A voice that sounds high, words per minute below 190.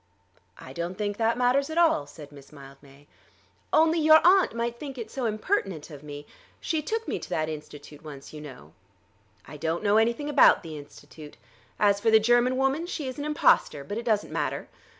No: high, 210 Hz; average, 195 wpm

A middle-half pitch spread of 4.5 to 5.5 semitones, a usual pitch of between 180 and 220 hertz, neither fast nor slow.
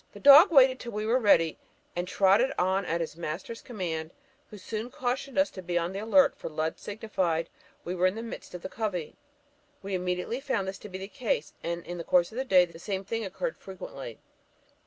No: average, 4.8 semitones; high, 190 Hz; fast, 220 wpm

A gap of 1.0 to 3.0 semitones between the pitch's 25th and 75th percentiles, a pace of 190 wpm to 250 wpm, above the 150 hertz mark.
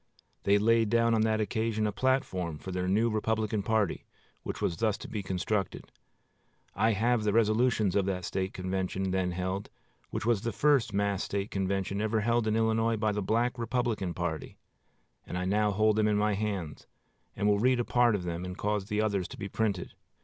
No: narrow, 2.6 semitones; average, 200 wpm; low, 105 Hz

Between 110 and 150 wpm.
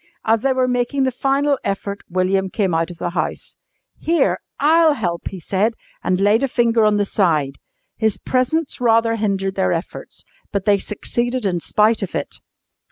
No: average, 175 wpm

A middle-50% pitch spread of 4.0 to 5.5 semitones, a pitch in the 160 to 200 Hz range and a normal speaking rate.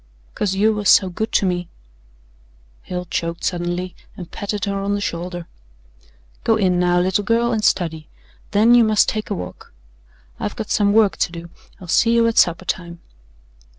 No: average, 3.2 semitones; high, 190 Hz; average, 180 wpm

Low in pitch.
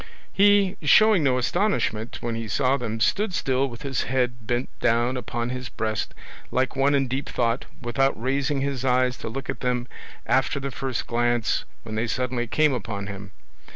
Yes: low, 125 Hz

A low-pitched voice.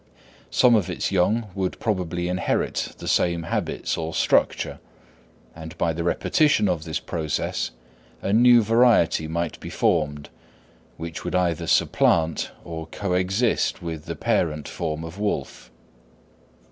Yes: very low, 85 Hz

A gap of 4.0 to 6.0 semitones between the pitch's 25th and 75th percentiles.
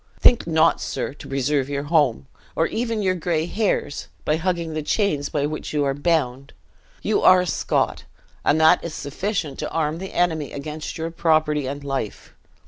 No: average, 3.2 semitones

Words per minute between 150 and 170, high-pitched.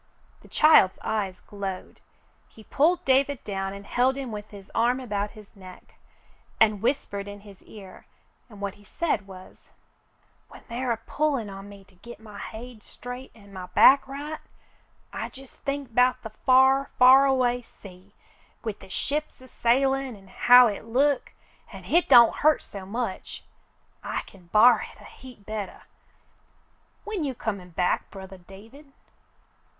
Yes: average, 165 wpm; high, 225 Hz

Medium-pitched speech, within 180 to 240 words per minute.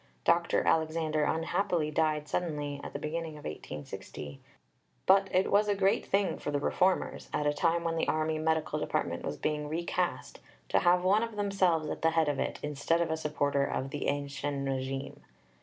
Yes: medium, 155 Hz; average, 185 wpm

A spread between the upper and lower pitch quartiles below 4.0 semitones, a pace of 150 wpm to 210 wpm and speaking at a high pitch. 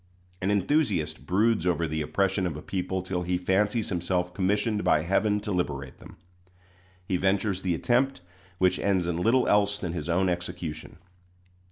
No: average, 2.8 semitones; average, 165 wpm; very low, 95 Hz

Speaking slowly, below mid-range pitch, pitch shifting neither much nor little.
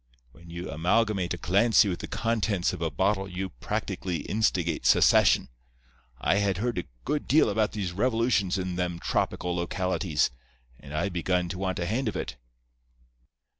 No: average, 165 wpm; very low, 95 Hz; average, 3.4 semitones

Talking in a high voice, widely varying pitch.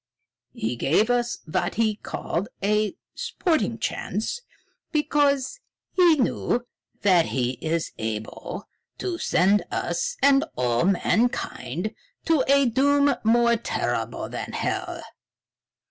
Yes: high, 235 Hz; wide, 8.1 semitones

